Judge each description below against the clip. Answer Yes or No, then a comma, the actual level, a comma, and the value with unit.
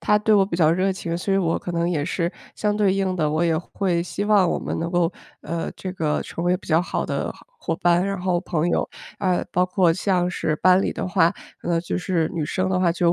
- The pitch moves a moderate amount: No, narrow, 2.1 semitones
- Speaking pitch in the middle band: Yes, medium, 180 Hz